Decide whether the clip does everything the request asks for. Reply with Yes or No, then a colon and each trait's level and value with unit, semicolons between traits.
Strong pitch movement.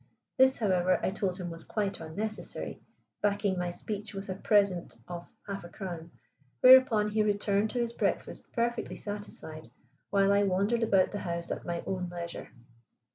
No: average, 3.0 semitones